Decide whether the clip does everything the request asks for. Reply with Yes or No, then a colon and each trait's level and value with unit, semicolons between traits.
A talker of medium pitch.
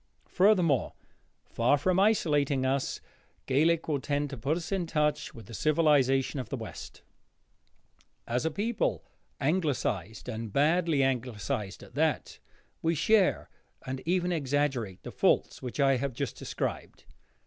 Yes: medium, 145 Hz